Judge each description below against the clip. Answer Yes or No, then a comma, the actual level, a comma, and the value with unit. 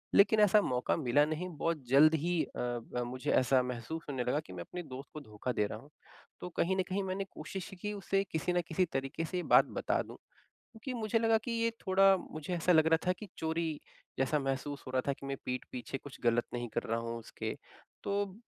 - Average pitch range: No, wide, 6.7 semitones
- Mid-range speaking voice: Yes, medium, 155 Hz